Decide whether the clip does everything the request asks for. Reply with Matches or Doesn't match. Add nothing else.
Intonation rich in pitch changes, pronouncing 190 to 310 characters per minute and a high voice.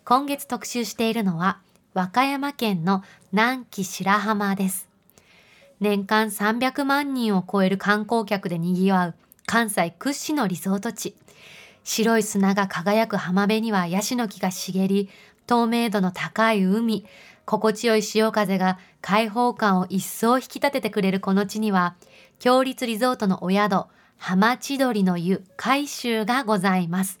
Doesn't match